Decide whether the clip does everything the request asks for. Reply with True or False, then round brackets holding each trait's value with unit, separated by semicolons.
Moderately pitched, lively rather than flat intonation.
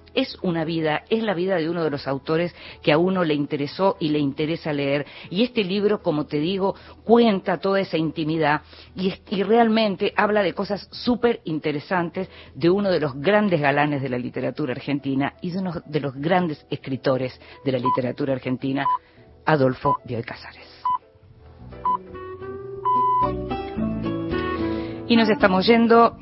True (170 Hz; 6.2 semitones)